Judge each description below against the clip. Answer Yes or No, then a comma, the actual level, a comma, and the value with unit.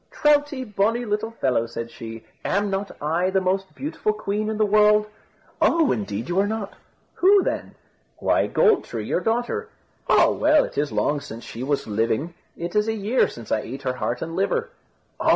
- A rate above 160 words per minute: Yes, average, 190 wpm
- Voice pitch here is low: No, high, 195 Hz